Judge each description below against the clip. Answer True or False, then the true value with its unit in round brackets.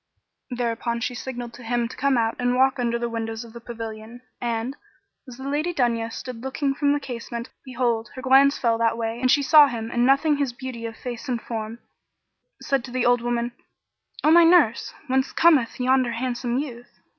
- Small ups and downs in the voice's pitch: True (2.3 semitones)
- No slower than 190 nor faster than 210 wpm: True (200 wpm)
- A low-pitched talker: False (245 Hz)